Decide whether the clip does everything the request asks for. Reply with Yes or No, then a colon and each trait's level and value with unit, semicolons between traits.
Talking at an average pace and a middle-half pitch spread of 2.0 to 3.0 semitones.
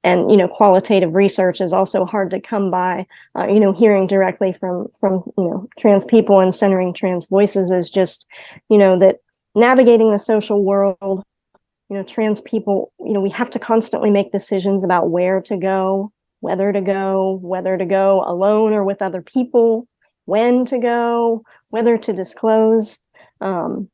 Yes: average, 175 wpm; narrow, 2.5 semitones